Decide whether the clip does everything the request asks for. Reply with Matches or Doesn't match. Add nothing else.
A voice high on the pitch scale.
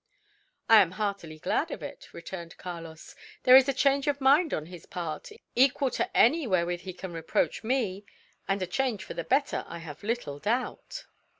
Matches